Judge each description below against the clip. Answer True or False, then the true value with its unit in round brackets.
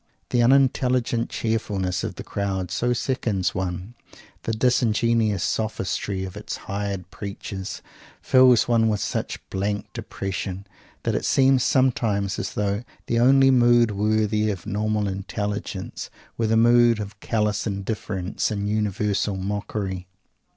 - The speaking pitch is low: True (105 Hz)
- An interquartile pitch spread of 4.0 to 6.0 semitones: False (3.0 semitones)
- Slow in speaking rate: True (130 wpm)